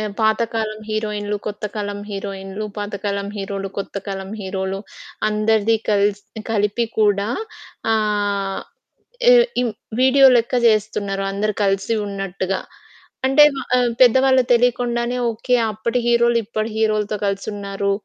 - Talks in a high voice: Yes, high, 210 Hz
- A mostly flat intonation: Yes, narrow, 2.3 semitones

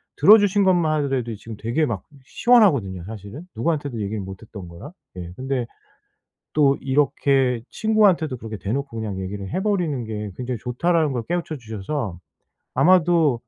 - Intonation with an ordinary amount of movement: No, wide, 6.8 semitones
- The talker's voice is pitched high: No, low, 130 Hz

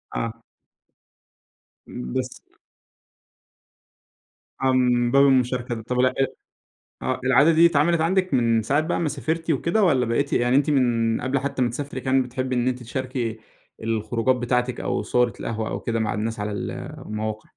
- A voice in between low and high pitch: No, low, 125 Hz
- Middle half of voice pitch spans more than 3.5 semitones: No, average, 3.2 semitones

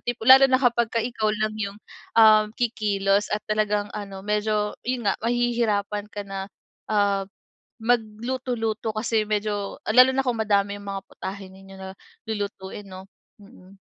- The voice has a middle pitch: No, high, 210 Hz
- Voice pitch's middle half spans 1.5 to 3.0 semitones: Yes, narrow, 2.4 semitones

